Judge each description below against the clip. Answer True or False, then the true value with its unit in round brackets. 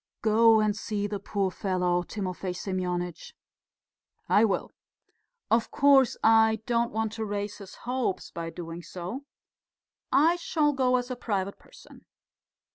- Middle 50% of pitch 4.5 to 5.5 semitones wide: False (4.1 semitones)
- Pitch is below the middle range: False (210 Hz)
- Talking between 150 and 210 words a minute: False (135 wpm)